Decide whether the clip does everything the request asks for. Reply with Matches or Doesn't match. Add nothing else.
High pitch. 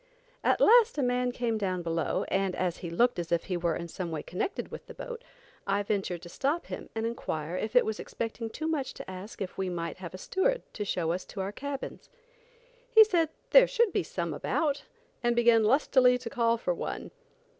Matches